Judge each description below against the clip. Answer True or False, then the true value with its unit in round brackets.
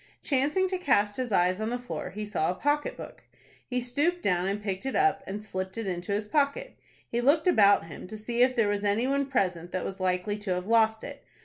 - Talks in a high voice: True (215 Hz)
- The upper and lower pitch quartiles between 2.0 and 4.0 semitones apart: False (5.6 semitones)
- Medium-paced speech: False (235 wpm)